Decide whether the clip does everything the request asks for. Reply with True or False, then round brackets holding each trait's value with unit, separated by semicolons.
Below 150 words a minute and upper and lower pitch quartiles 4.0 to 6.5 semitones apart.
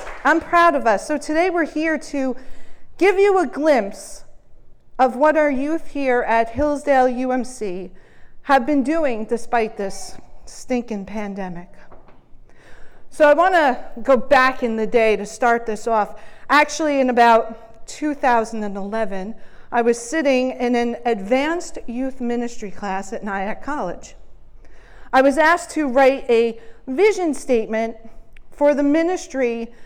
True (135 wpm; 4.7 semitones)